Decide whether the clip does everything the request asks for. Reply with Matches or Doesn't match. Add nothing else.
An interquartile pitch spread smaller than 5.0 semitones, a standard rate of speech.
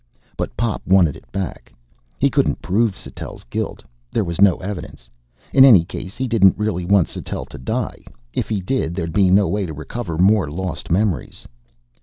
Matches